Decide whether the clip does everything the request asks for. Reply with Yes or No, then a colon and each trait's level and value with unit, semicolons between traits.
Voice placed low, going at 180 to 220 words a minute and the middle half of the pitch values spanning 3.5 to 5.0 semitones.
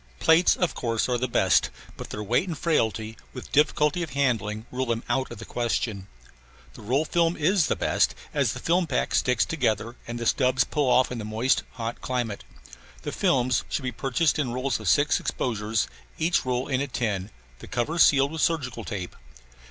Yes: low, 125 Hz; average, 195 wpm; average, 4.3 semitones